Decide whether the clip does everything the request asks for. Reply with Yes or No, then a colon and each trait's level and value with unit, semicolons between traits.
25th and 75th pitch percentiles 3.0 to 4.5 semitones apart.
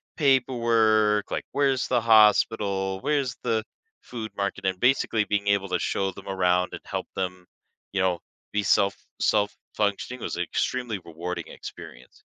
Yes: average, 3.4 semitones